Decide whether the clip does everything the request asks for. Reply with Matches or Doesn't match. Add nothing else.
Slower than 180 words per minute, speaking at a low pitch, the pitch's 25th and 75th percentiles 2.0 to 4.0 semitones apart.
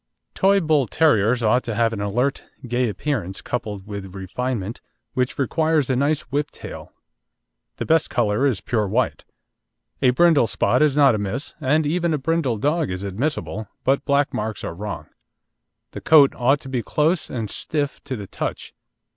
Doesn't match